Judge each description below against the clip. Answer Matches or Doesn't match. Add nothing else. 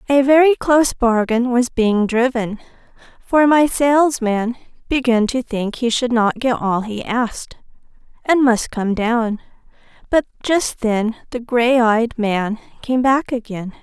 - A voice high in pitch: Matches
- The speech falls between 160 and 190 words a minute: Doesn't match